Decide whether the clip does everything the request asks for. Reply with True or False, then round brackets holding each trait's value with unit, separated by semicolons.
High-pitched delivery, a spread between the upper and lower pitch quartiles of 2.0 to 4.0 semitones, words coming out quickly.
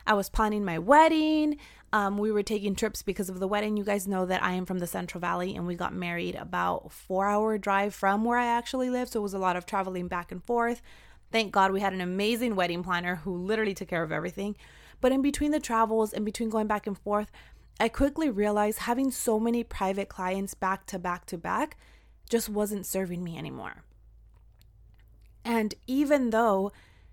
True (205 Hz; 3.6 semitones; 210 wpm)